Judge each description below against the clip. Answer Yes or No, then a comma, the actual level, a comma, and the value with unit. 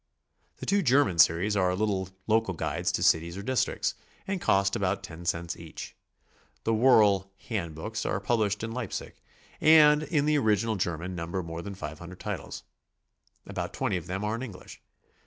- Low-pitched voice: Yes, low, 100 Hz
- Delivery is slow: No, average, 175 wpm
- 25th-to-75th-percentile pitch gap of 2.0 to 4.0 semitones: No, average, 4.4 semitones